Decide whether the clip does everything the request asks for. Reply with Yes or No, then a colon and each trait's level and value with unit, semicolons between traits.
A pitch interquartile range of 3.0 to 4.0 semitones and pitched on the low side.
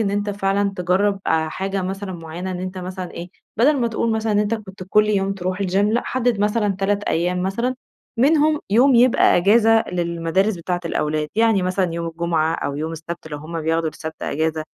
No: average, 3.7 semitones; high, 190 Hz